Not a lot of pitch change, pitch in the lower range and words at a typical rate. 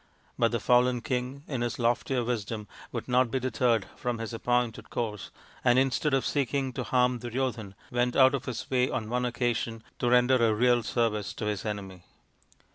Yes: narrow, 1.9 semitones; low, 120 Hz; average, 185 wpm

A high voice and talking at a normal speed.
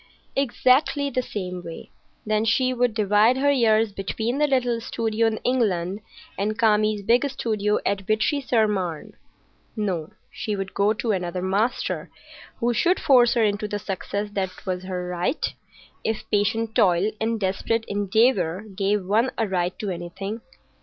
Yes: high, 215 Hz; average, 155 wpm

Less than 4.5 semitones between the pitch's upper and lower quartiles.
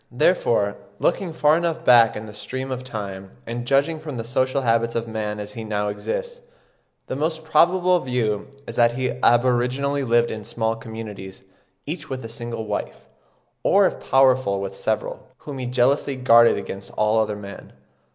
Yes: average, 4.1 semitones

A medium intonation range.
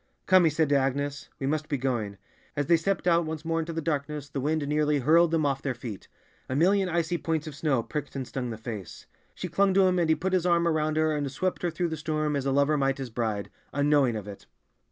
Yes: average, 3.4 semitones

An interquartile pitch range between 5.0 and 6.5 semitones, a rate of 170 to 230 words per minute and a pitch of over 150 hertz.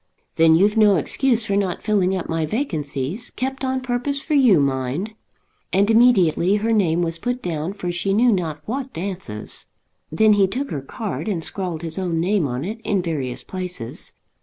Yes: average, 5.3 semitones; average, 185 wpm; high, 190 Hz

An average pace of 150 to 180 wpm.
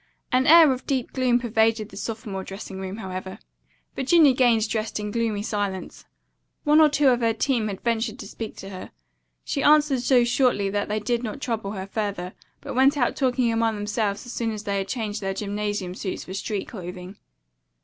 No: average, 190 wpm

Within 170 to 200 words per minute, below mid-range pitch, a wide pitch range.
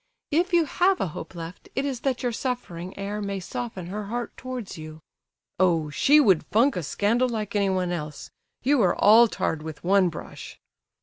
No: average, 185 wpm; high, 205 Hz; wide, 6.1 semitones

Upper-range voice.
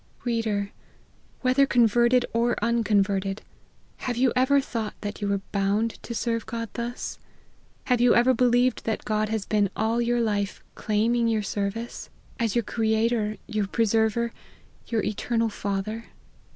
Yes: high, 225 Hz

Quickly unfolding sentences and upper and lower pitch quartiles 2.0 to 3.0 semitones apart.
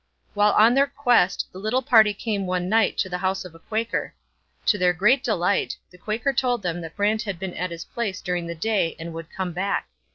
No: fast, 225 wpm; average, 3.8 semitones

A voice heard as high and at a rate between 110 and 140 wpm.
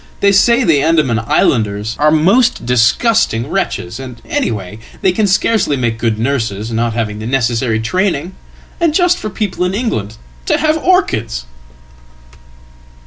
No: low, 135 Hz; slow, 135 wpm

